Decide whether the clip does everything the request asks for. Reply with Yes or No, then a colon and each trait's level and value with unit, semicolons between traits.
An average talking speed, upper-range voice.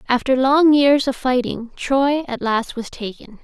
Yes: average, 175 wpm; very high, 255 Hz